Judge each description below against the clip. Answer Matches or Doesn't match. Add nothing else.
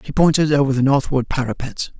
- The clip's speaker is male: Matches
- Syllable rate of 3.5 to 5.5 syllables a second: Doesn't match